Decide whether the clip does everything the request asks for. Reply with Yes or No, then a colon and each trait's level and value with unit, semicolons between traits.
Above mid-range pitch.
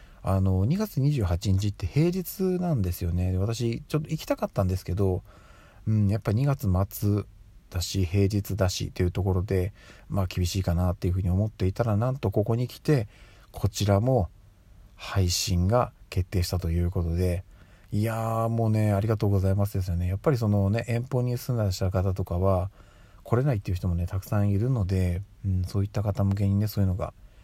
No: low, 100 Hz